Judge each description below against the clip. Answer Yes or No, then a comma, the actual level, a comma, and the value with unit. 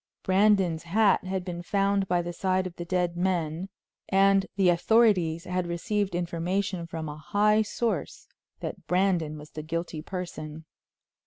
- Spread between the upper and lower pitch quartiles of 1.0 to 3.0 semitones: Yes, average, 2.7 semitones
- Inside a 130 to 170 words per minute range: Yes, average, 150 wpm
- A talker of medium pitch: Yes, medium, 180 Hz